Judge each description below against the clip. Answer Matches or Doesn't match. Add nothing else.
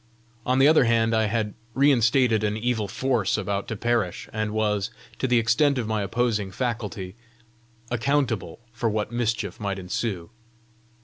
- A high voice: Doesn't match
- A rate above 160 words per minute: Doesn't match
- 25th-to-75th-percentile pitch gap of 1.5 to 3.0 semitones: Matches